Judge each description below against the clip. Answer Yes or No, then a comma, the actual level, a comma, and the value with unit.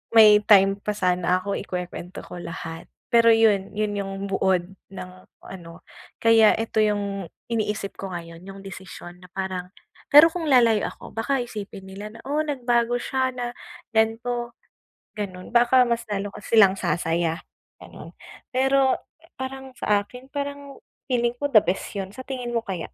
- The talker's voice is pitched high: Yes, high, 215 Hz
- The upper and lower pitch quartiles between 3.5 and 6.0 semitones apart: Yes, average, 4.1 semitones